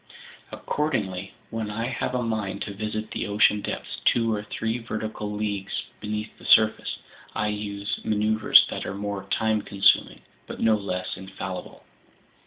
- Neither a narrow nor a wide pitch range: No, narrow, 1.5 semitones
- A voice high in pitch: No, low, 105 Hz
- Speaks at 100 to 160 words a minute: Yes, average, 150 wpm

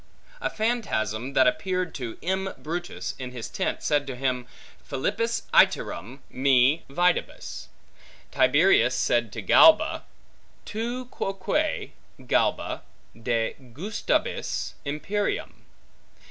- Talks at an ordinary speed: No, slow, 95 wpm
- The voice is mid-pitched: Yes, medium, 155 Hz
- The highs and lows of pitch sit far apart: Yes, wide, 8.2 semitones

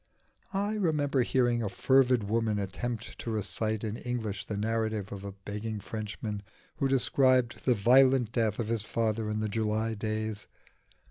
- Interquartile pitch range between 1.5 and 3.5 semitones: Yes, narrow, 2.6 semitones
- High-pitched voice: No, low, 110 Hz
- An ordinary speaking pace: Yes, average, 155 wpm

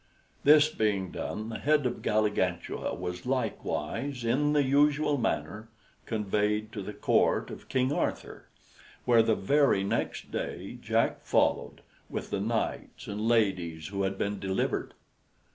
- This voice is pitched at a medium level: No, low, 110 Hz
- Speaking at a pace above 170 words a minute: No, average, 140 wpm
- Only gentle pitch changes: No, wide, 5.4 semitones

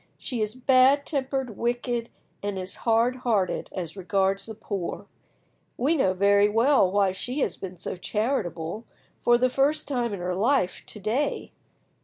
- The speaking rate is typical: Yes, average, 160 wpm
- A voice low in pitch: No, high, 225 Hz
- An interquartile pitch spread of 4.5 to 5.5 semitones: Yes, average, 4.9 semitones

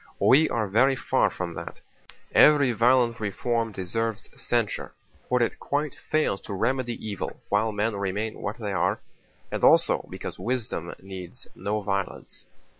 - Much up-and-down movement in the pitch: No, average, 3.8 semitones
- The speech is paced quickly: No, average, 145 wpm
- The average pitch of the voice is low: Yes, low, 110 Hz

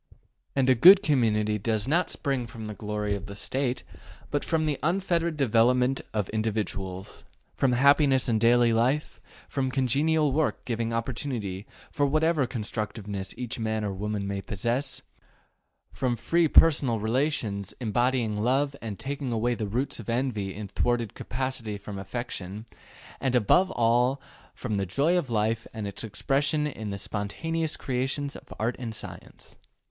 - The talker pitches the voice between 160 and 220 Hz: No, low, 120 Hz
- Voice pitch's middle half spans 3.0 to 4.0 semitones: No, average, 4.4 semitones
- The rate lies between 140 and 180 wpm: Yes, average, 150 wpm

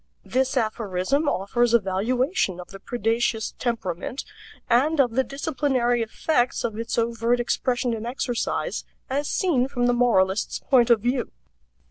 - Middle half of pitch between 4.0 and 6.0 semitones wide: No, narrow, 2.4 semitones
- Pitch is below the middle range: No, high, 240 Hz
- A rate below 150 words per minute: Yes, average, 140 wpm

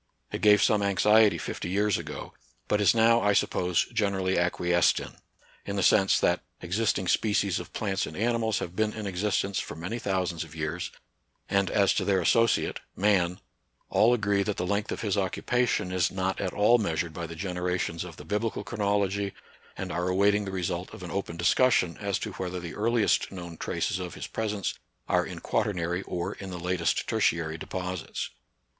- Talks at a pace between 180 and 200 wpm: Yes, average, 190 wpm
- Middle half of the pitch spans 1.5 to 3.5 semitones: Yes, average, 2.7 semitones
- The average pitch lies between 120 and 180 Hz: No, very low, 95 Hz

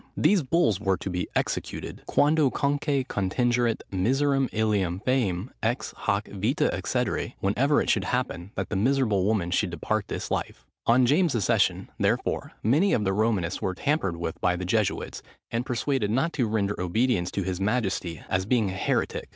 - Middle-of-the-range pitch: No, low, 110 Hz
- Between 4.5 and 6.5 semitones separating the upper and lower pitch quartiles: Yes, average, 5.3 semitones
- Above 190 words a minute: No, average, 165 wpm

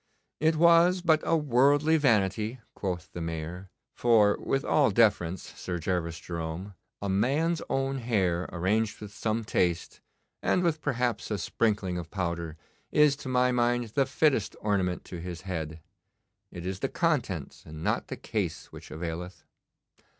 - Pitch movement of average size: No, wide, 7.3 semitones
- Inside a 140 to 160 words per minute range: Yes, average, 150 wpm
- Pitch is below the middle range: Yes, low, 105 Hz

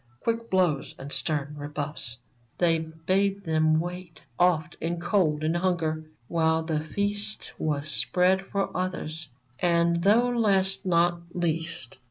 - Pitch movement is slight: No, average, 3.0 semitones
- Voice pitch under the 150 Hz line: No, medium, 170 Hz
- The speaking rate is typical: No, slow, 130 wpm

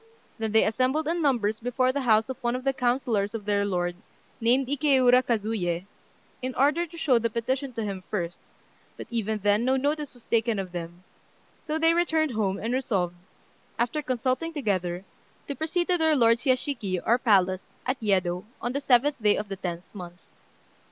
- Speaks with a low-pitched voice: No, high, 235 Hz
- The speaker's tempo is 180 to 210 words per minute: Yes, average, 185 wpm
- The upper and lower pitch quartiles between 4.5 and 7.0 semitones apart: Yes, average, 5.0 semitones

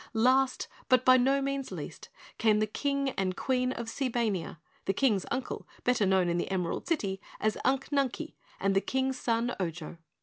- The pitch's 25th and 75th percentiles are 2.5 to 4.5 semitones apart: No, average, 5.3 semitones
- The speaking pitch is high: Yes, high, 245 Hz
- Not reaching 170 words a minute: No, average, 175 wpm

